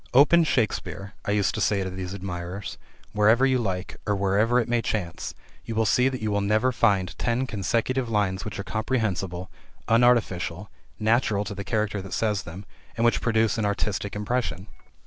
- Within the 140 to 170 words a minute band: No, average, 180 wpm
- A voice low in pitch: Yes, low, 105 Hz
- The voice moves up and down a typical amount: Yes, average, 3.1 semitones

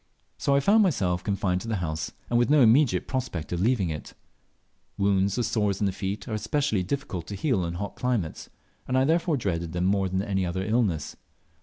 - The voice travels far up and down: Yes, wide, 5.7 semitones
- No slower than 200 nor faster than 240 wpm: Yes, fast, 205 wpm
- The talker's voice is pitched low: Yes, low, 100 Hz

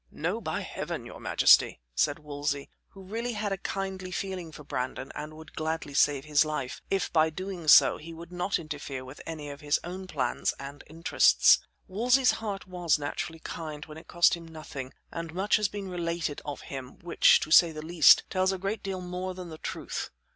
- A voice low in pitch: No, medium, 165 Hz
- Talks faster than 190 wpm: Yes, average, 200 wpm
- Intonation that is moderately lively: Yes, average, 3.9 semitones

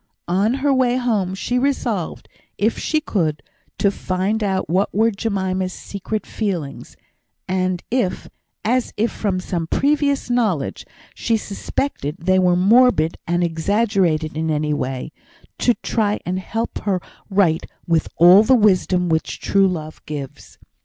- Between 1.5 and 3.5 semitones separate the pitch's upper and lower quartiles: No, average, 4.7 semitones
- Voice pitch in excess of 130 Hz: Yes, high, 190 Hz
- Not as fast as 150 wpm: Yes, average, 140 wpm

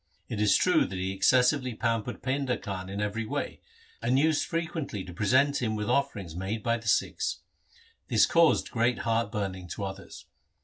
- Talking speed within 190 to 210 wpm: No, average, 180 wpm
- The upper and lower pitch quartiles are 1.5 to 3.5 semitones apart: No, average, 4.7 semitones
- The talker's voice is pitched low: Yes, low, 115 Hz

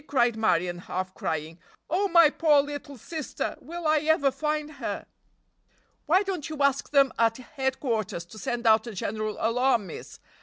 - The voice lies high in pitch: Yes, very high, 265 Hz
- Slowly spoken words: No, average, 160 wpm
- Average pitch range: No, wide, 5.8 semitones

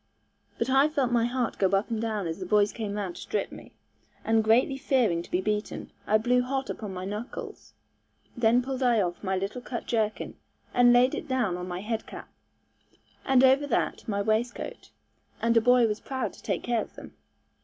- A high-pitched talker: Yes, high, 230 Hz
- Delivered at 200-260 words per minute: Yes, fast, 205 wpm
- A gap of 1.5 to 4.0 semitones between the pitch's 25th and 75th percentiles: Yes, average, 3.3 semitones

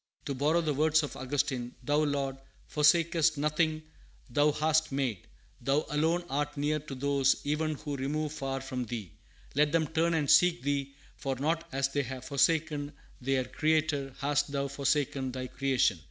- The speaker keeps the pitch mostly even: Yes, narrow, 2.3 semitones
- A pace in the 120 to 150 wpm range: No, average, 165 wpm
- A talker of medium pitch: Yes, medium, 145 Hz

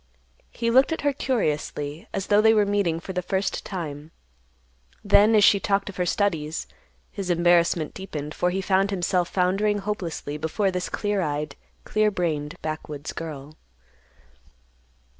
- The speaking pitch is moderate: Yes, medium, 180 Hz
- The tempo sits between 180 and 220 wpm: No, average, 150 wpm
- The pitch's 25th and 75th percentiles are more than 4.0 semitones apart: Yes, average, 4.5 semitones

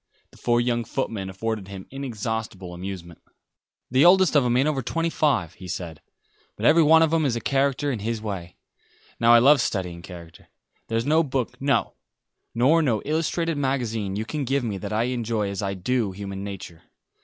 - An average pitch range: No, wide, 5.9 semitones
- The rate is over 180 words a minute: Yes, average, 190 wpm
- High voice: No, low, 115 Hz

